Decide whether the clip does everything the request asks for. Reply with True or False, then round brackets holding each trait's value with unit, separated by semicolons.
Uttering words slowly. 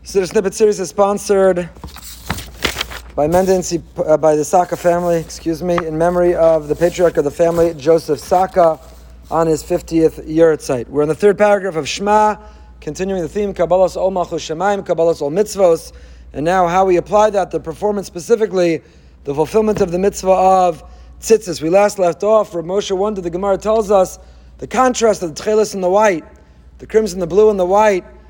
False (190 wpm)